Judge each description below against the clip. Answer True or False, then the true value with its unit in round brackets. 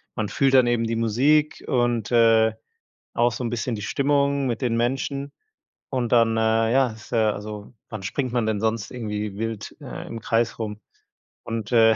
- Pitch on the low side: True (115 Hz)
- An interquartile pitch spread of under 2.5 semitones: True (2.1 semitones)